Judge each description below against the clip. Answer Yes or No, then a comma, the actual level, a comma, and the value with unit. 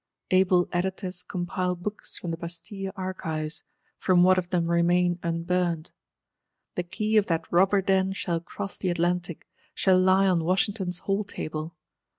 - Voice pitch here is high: No, medium, 180 Hz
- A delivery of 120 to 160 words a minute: Yes, average, 155 wpm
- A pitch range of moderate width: No, narrow, 1.7 semitones